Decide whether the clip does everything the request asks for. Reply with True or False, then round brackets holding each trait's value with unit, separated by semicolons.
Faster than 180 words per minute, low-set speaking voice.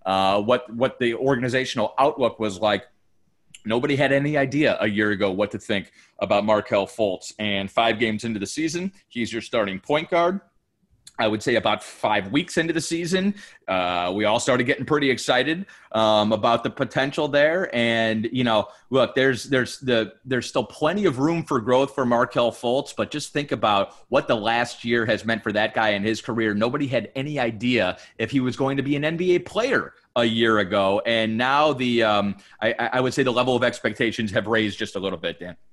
True (205 wpm; 120 Hz)